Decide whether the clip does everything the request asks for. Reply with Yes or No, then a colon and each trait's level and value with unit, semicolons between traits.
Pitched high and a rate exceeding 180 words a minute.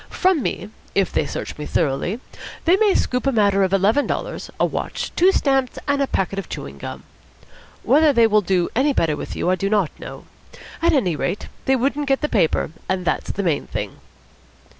Yes: high, 215 Hz; fast, 205 wpm